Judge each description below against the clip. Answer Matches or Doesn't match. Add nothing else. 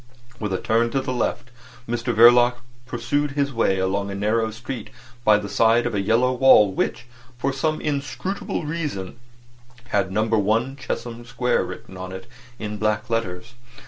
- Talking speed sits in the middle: Matches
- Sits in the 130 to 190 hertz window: Doesn't match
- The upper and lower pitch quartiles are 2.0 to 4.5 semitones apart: Matches